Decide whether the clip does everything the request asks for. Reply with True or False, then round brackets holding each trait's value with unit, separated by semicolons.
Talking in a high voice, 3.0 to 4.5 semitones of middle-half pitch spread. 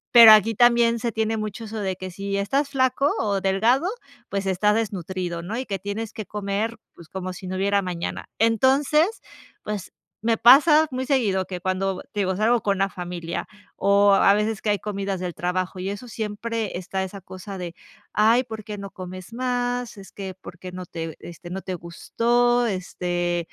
True (200 Hz; 3.6 semitones)